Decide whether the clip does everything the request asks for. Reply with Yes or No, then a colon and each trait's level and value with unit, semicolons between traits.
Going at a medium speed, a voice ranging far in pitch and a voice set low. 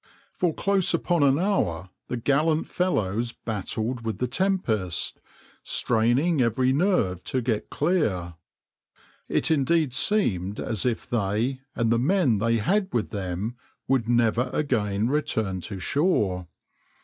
No: slow, 130 wpm; wide, 6.5 semitones; low, 120 Hz